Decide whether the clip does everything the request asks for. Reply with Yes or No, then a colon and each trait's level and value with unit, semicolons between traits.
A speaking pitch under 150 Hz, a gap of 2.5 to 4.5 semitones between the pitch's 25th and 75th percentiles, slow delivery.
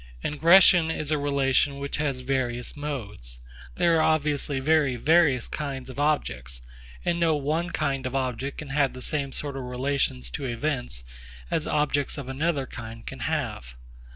No: medium, 140 Hz; average, 3.0 semitones; average, 160 wpm